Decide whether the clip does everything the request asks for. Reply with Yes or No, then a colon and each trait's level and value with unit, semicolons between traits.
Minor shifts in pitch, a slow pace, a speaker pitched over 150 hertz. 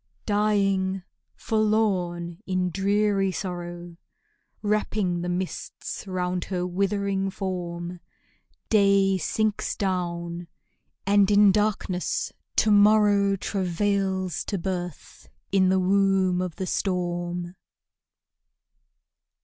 Yes: narrow, 2.1 semitones; slow, 90 wpm; high, 190 Hz